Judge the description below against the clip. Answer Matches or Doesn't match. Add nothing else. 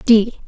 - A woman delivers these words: Matches